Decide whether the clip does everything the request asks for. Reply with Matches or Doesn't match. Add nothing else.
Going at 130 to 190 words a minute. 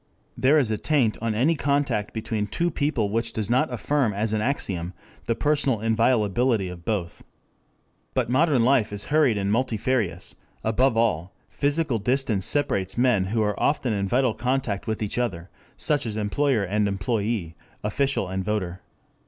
Matches